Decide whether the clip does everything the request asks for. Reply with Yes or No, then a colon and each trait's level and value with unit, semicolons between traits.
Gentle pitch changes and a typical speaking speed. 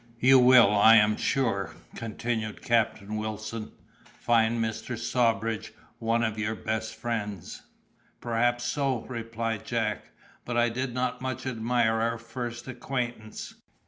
No: narrow, 1.6 semitones; slow, 125 wpm